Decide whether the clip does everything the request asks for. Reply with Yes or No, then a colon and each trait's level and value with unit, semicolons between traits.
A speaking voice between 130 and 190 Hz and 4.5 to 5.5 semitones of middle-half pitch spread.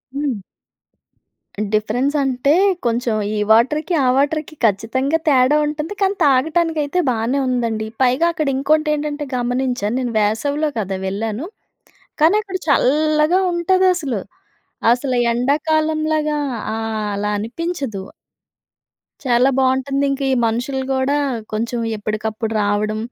No: very high, 265 Hz; average, 4.9 semitones